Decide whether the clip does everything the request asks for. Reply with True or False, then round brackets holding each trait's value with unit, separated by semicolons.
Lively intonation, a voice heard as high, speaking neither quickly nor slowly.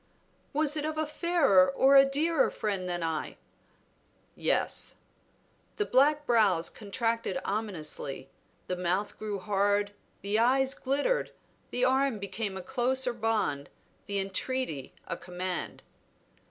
False (6.2 semitones; 220 Hz; 125 wpm)